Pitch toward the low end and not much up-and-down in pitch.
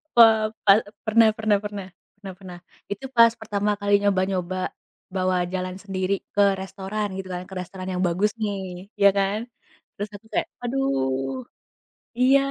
No: high, 195 Hz; narrow, 2.2 semitones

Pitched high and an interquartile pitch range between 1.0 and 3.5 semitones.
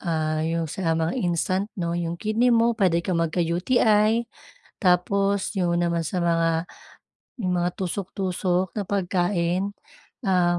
No: medium, 180 Hz; average, 2.7 semitones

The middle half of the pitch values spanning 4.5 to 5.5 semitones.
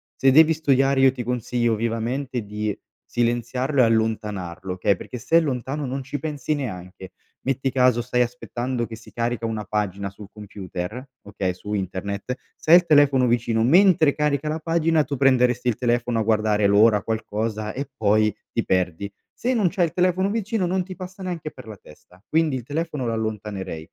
Yes: average, 5.2 semitones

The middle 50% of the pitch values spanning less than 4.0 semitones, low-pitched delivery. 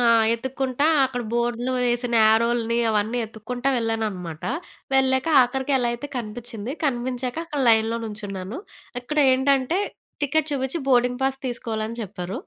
No: average, 2.9 semitones; high, 240 Hz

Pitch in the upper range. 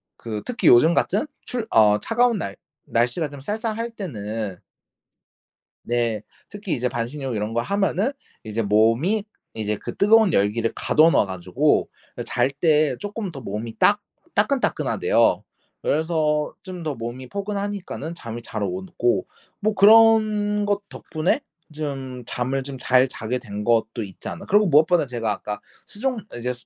No: medium, 140 Hz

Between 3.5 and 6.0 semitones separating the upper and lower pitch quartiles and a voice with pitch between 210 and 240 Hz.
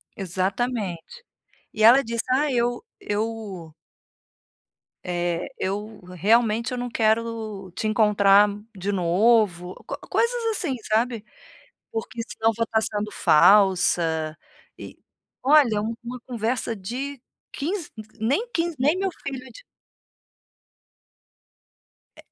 Yes: average, 3.9 semitones; high, 220 Hz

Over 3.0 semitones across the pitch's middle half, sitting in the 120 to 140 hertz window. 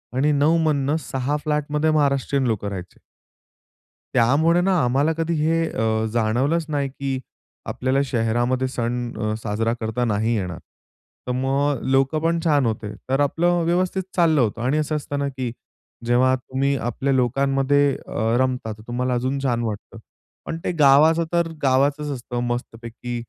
Yes: average, 3.5 semitones; low, 135 Hz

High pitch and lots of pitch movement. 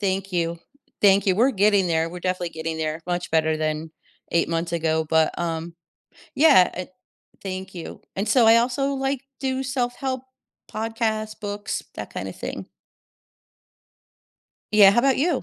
Yes: high, 195 Hz; wide, 5.8 semitones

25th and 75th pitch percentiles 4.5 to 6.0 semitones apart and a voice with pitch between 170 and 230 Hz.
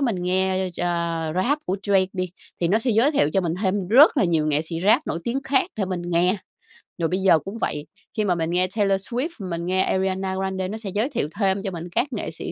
No: average, 3.5 semitones; high, 190 Hz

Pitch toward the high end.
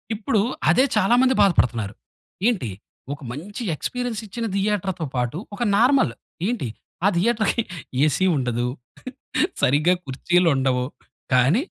No: medium, 180 Hz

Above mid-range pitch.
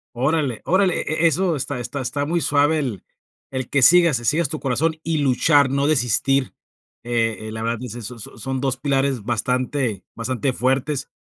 No: low, 135 Hz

